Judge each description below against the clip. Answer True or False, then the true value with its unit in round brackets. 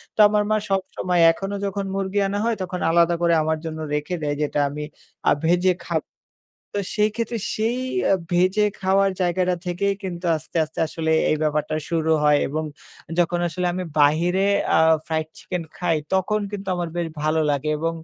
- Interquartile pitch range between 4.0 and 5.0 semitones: False (3.5 semitones)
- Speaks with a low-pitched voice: False (175 Hz)